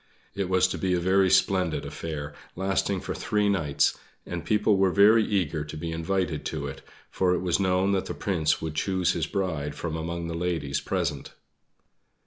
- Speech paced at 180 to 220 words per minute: Yes, average, 185 wpm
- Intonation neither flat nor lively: Yes, average, 3.3 semitones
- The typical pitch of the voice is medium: No, very low, 90 Hz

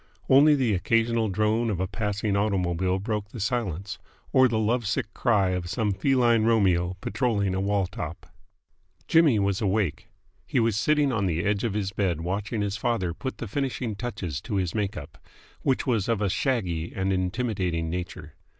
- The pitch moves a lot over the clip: No, average, 3.8 semitones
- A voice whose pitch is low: Yes, low, 105 Hz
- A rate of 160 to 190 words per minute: Yes, average, 180 wpm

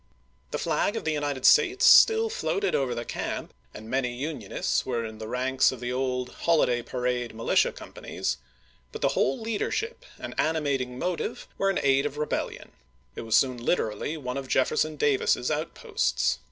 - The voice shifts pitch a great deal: No, average, 4.2 semitones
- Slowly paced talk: No, average, 165 wpm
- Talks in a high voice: No, low, 135 Hz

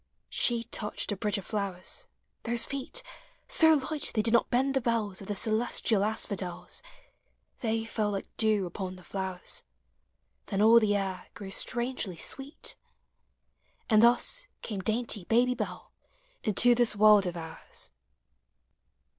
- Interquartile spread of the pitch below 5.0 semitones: Yes, average, 3.4 semitones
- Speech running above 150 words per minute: No, average, 140 wpm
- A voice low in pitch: No, high, 215 Hz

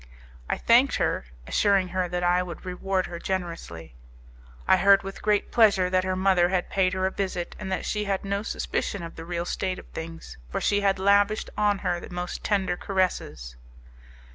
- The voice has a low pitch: No, medium, 185 Hz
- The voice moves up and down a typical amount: No, narrow, 2.0 semitones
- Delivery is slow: No, average, 190 wpm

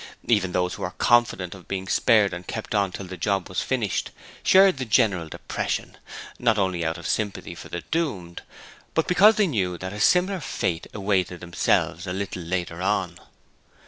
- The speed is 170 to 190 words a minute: Yes, average, 180 wpm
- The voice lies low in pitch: Yes, very low, 95 Hz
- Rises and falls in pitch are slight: No, average, 4.8 semitones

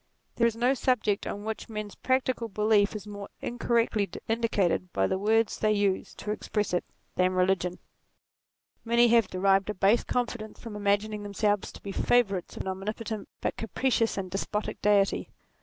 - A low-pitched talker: No, high, 210 Hz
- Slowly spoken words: No, average, 170 wpm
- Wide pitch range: No, narrow, 2.6 semitones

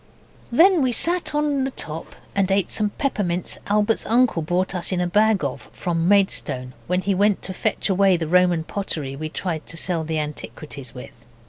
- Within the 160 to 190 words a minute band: Yes, average, 185 wpm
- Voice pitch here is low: No, medium, 185 Hz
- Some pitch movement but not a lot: Yes, average, 4.6 semitones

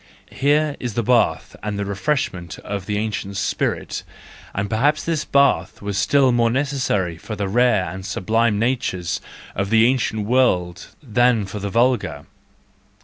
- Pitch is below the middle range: Yes, low, 110 Hz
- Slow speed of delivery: No, average, 155 wpm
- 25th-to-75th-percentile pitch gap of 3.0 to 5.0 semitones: Yes, average, 4.4 semitones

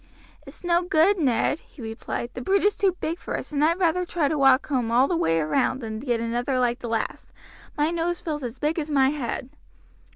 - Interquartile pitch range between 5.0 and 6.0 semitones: Yes, wide, 5.5 semitones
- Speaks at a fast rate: Yes, fast, 225 wpm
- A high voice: Yes, very high, 285 Hz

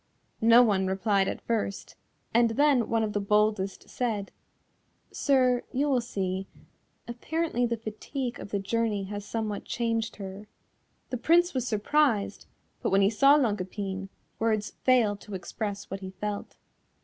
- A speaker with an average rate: Yes, average, 150 wpm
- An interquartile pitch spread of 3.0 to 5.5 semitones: Yes, average, 3.5 semitones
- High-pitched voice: Yes, high, 215 Hz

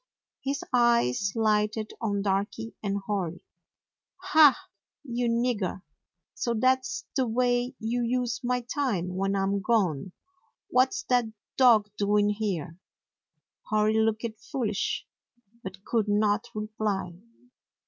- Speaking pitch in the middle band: No, high, 215 Hz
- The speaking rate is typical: No, slow, 115 wpm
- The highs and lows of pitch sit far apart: No, average, 3.3 semitones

